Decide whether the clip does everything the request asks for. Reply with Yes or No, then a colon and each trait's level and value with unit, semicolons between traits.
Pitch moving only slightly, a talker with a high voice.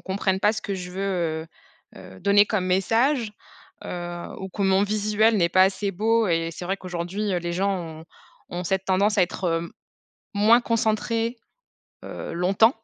No: average, 3.1 semitones; high, 195 Hz